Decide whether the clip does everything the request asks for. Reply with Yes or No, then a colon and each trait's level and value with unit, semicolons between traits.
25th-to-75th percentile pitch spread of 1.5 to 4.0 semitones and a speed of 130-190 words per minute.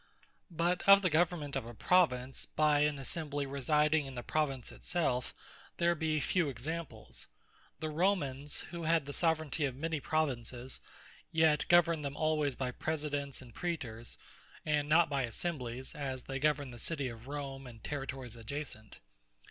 Yes: average, 3.5 semitones; average, 155 wpm